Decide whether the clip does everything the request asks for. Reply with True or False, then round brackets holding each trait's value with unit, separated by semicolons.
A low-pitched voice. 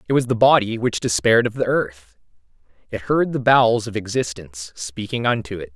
True (115 Hz)